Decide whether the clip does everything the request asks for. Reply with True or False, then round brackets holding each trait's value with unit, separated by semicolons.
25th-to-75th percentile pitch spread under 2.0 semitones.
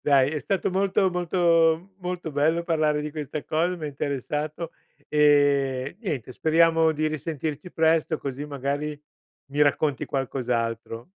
False (2.7 semitones)